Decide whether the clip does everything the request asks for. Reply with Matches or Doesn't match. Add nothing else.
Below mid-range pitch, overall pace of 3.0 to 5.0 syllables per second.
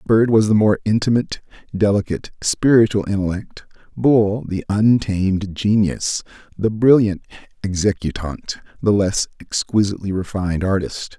Matches